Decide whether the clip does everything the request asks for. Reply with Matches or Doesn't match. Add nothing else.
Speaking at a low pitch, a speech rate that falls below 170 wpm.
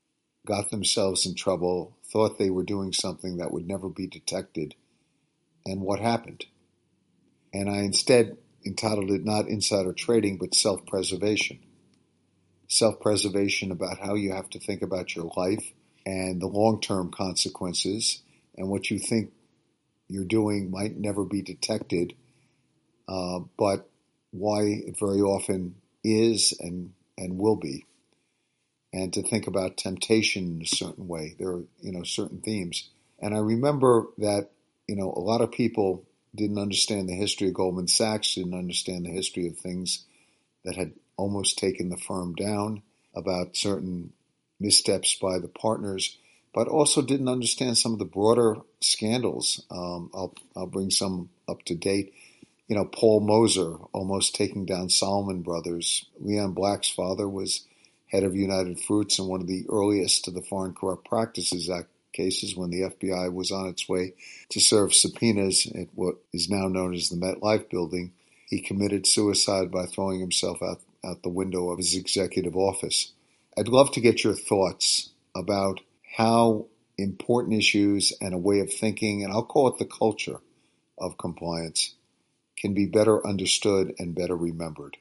Matches